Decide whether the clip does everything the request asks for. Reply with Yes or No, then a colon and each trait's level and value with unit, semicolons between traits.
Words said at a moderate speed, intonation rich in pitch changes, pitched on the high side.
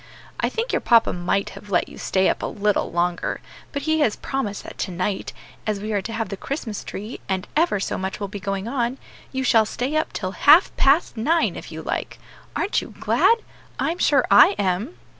No: fast, 210 wpm; wide, 6.0 semitones; high, 220 Hz